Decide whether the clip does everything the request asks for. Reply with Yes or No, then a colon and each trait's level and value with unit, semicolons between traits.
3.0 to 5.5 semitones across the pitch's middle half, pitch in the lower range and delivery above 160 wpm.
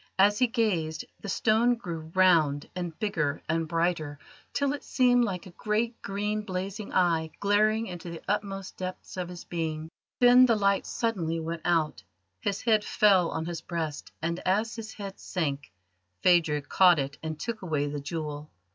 No: average, 4.7 semitones; medium, 180 Hz; average, 170 wpm